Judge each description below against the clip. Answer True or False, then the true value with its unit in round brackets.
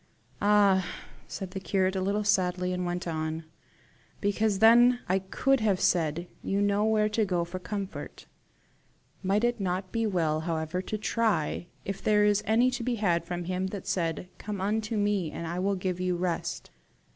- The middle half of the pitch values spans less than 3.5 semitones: True (2.9 semitones)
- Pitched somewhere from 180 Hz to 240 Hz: True (190 Hz)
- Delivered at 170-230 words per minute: True (180 wpm)